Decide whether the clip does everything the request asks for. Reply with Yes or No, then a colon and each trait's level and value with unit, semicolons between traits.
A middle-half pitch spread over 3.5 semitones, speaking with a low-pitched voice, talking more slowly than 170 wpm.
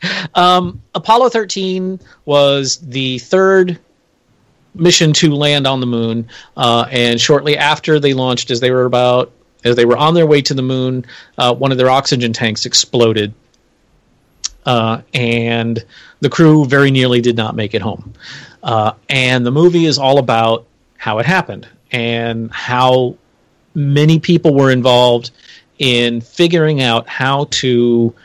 Yes: average, 4.0 semitones; low, 130 Hz; average, 150 wpm